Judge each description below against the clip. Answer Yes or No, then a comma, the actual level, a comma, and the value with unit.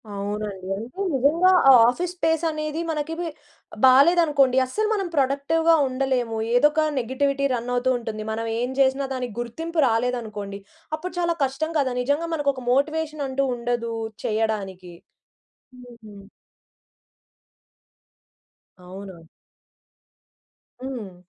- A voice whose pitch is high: Yes, very high, 260 Hz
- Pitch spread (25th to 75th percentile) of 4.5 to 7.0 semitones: Yes, average, 5.1 semitones